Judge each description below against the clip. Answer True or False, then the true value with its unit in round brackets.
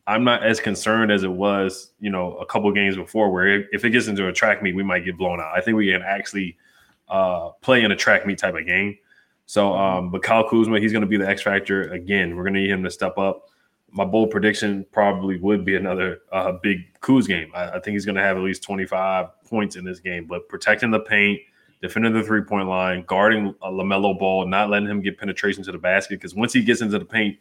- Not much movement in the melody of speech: True (2.1 semitones)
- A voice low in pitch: True (100 Hz)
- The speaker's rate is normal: False (250 wpm)